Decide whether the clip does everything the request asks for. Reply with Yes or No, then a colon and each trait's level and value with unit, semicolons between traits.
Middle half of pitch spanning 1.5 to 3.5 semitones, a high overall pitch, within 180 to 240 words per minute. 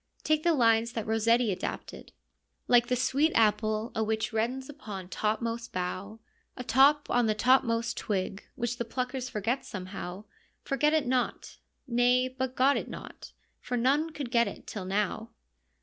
No: average, 3.1 semitones; high, 235 Hz; average, 165 wpm